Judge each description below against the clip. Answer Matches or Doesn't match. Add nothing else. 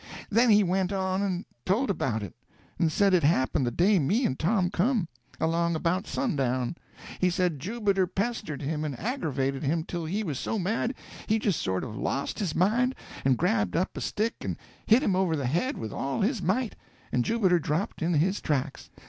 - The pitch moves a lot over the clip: Matches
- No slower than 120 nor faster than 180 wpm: Doesn't match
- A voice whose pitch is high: Doesn't match